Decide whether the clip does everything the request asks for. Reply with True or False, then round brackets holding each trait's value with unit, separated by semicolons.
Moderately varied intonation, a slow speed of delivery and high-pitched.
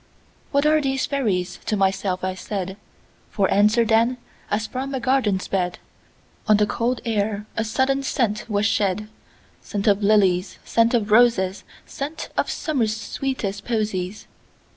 True (3.6 semitones; 130 wpm; 215 Hz)